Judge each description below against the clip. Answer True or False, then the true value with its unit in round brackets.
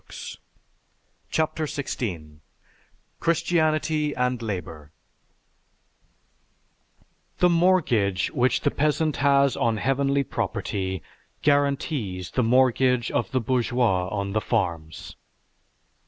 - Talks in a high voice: False (125 Hz)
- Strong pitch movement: True (6.5 semitones)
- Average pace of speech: False (90 wpm)